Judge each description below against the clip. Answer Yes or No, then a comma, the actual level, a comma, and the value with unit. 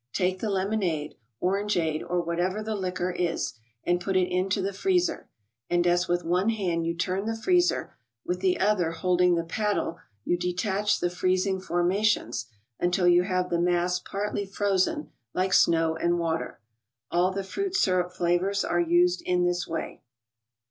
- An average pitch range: No, narrow, 2.0 semitones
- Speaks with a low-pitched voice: No, medium, 180 Hz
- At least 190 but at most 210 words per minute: No, average, 165 wpm